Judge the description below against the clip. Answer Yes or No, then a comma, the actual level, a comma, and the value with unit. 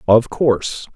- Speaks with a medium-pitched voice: No, low, 120 Hz